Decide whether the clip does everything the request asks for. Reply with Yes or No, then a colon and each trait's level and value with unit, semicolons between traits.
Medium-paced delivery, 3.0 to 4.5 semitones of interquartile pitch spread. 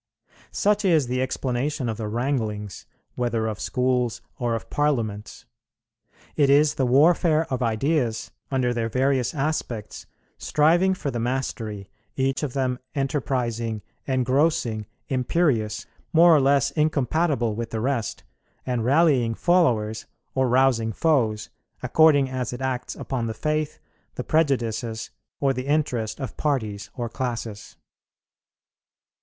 No: slow, 125 wpm; average, 4.0 semitones